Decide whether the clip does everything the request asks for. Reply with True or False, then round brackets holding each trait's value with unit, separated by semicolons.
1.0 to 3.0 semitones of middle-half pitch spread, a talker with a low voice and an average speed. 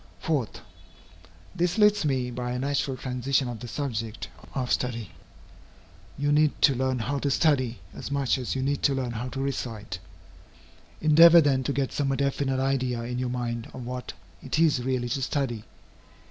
True (2.4 semitones; 130 Hz; 175 wpm)